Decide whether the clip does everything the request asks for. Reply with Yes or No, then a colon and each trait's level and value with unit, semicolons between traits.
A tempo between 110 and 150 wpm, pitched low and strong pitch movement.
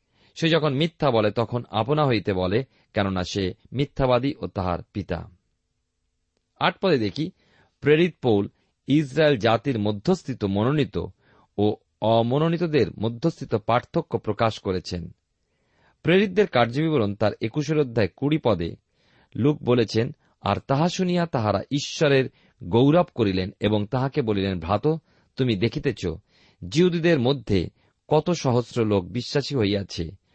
Yes: average, 115 wpm; low, 120 Hz; wide, 6.4 semitones